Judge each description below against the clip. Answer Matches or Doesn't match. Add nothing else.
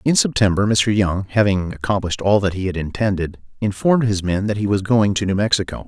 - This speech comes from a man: Matches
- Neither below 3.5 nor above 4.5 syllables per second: Doesn't match